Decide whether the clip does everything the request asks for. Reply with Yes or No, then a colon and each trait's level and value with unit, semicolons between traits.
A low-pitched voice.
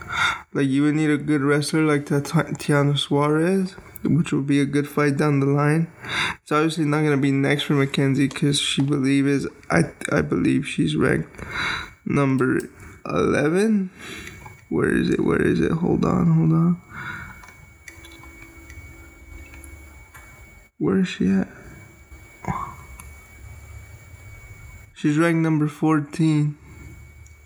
No: medium, 145 Hz